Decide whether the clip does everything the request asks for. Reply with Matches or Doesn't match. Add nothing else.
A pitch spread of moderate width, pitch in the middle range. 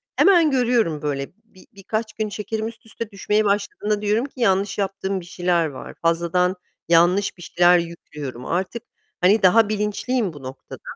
Doesn't match